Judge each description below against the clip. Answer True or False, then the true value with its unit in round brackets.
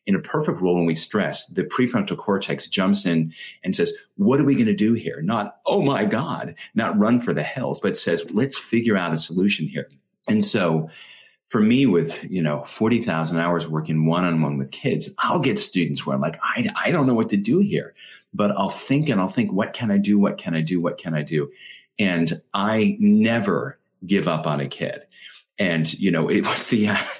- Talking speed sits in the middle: False (220 wpm)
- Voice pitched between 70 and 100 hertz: True (95 Hz)